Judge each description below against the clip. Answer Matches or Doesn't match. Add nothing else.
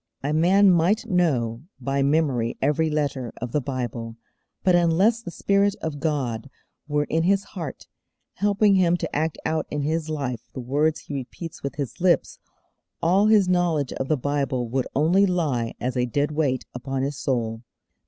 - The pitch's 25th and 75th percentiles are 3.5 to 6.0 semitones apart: Matches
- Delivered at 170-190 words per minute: Matches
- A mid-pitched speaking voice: Matches